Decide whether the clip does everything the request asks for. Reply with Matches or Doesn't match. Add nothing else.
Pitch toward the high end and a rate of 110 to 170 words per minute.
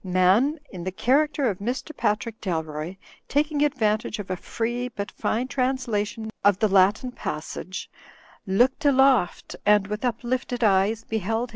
Matches